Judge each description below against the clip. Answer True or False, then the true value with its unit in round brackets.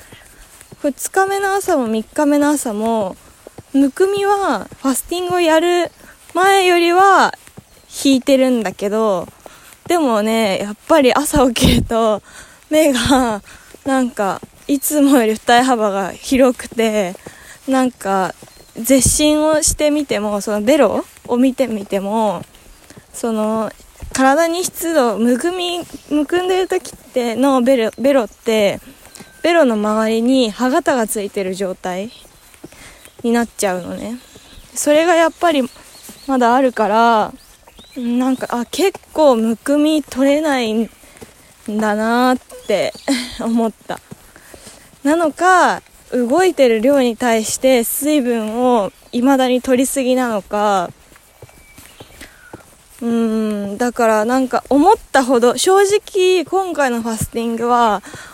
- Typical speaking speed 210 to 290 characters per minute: True (225 characters per minute)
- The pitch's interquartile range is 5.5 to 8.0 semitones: False (5.1 semitones)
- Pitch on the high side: True (255 Hz)